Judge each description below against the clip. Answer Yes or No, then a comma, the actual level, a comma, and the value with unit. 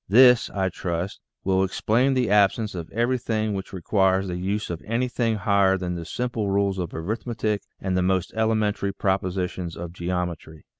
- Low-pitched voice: Yes, low, 100 Hz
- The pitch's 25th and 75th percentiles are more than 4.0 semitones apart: No, average, 3.2 semitones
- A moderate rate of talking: Yes, average, 165 wpm